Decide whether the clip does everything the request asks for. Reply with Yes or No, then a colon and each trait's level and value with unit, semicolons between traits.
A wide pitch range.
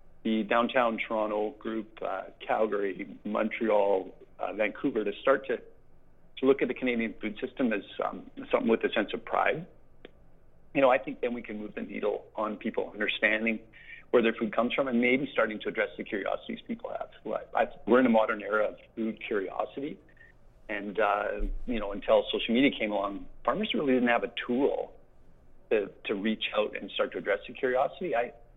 No: average, 3.4 semitones